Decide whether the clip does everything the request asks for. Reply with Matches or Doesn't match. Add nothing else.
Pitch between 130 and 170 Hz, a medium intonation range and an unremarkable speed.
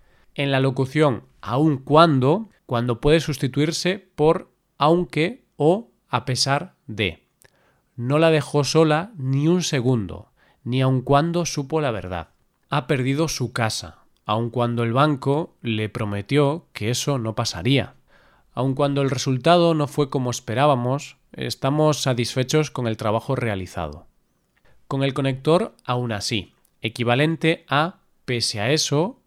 Matches